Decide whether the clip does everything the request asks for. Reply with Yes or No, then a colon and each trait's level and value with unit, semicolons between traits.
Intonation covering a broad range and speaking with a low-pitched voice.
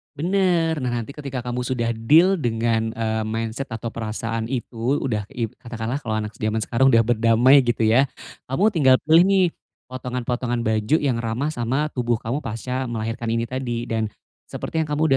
No: average, 3.1 semitones; low, 120 Hz